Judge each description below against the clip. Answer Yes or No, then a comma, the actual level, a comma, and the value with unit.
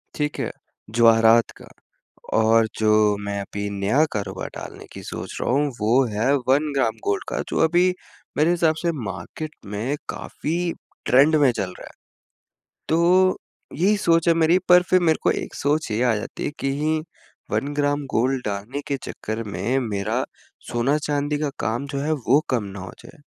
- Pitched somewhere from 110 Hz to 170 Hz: Yes, medium, 140 Hz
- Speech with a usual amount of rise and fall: No, wide, 6.0 semitones